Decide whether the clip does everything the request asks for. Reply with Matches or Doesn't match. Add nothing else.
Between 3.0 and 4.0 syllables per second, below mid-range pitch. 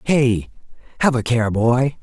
Matches